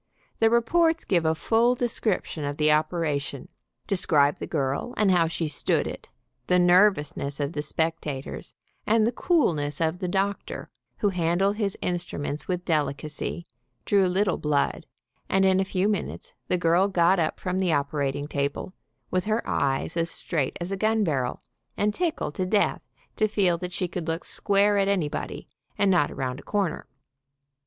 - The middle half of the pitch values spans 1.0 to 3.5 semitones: No, average, 4.8 semitones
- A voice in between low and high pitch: Yes, medium, 175 Hz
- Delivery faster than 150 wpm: Yes, average, 170 wpm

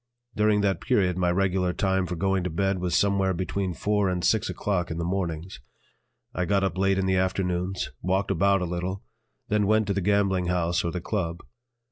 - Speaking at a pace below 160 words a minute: No, average, 200 wpm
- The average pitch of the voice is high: No, very low, 95 Hz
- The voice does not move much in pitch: Yes, narrow, 1.8 semitones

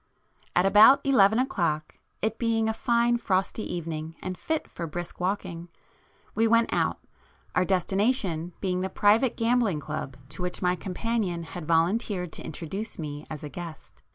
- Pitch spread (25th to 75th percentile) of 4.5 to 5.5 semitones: Yes, average, 4.9 semitones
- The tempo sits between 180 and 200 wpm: No, average, 155 wpm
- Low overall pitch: No, medium, 185 Hz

